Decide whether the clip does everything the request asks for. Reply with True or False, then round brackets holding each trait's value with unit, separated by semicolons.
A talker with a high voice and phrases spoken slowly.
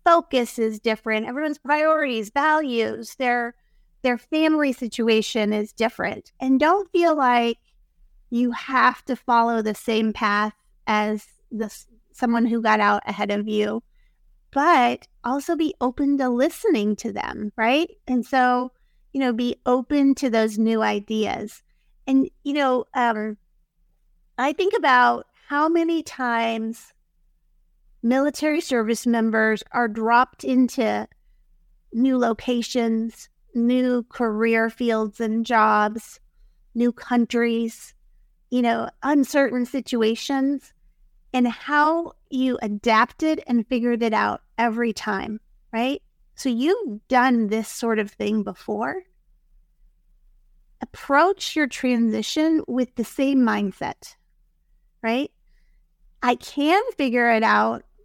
True (240 Hz; 115 wpm)